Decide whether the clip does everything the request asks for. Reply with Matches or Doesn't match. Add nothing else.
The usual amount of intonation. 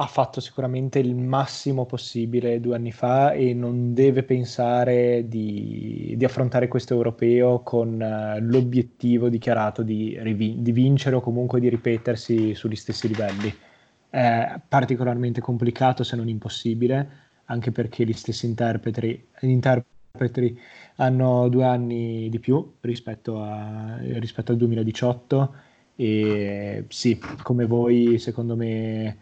Doesn't match